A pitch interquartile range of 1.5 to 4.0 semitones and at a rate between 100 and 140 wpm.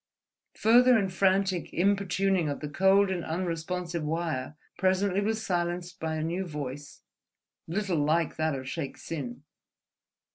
Yes: average, 3.5 semitones; slow, 135 wpm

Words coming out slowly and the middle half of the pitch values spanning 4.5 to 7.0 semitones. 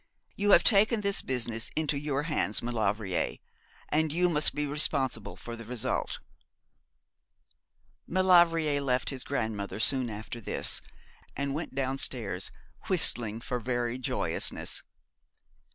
Yes: slow, 120 wpm; average, 4.9 semitones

